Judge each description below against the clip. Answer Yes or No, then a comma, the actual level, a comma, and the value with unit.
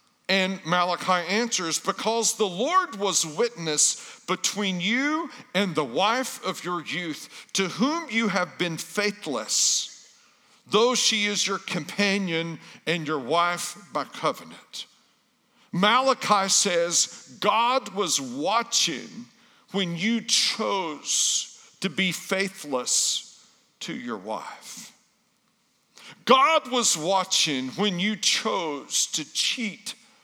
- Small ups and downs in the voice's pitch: No, average, 4.7 semitones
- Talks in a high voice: Yes, high, 200 Hz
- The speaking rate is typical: No, slow, 105 wpm